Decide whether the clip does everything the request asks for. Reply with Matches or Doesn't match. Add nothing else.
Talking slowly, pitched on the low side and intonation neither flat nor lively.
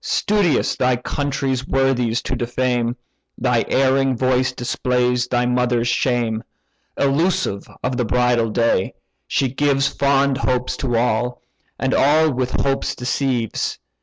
Doesn't match